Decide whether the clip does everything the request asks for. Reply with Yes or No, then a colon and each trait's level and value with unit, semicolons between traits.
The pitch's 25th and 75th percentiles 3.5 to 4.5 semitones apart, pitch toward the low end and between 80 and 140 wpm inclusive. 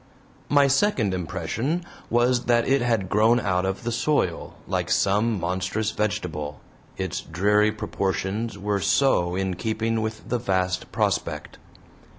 Yes: average, 4.0 semitones; low, 105 Hz; slow, 135 wpm